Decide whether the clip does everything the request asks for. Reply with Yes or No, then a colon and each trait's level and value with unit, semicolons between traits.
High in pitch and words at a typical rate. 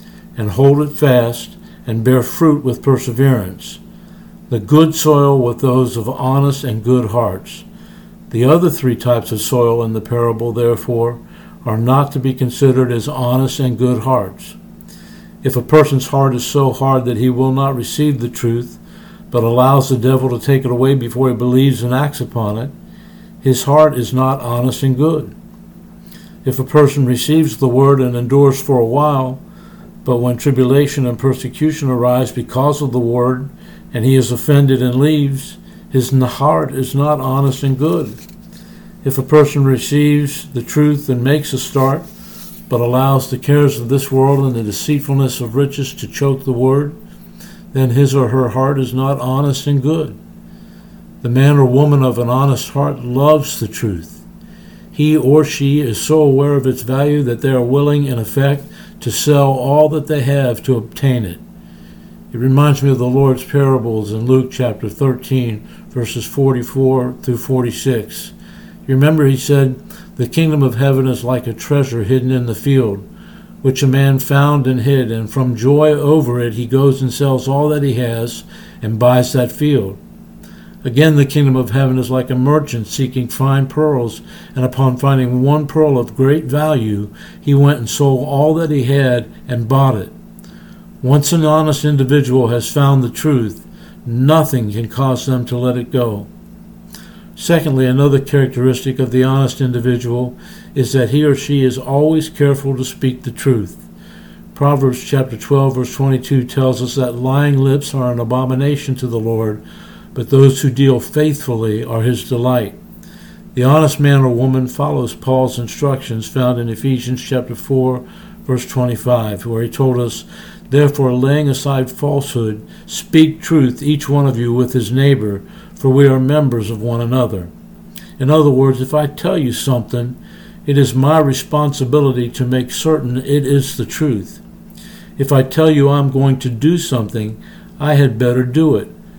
No: low, 135 Hz; average, 170 wpm